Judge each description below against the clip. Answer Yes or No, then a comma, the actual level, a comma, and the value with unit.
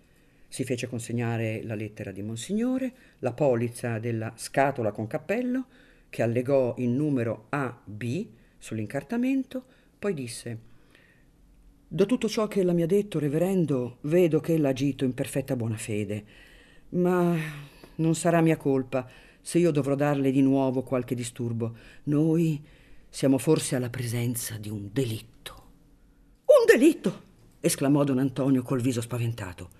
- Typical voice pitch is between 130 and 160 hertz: Yes, low, 135 Hz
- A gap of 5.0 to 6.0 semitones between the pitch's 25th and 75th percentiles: Yes, wide, 5.5 semitones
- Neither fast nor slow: Yes, average, 135 wpm